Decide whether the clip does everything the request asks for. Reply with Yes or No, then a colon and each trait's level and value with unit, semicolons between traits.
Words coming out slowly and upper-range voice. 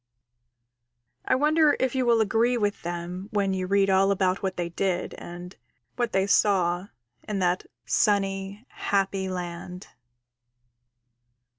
Yes: slow, 130 wpm; high, 195 Hz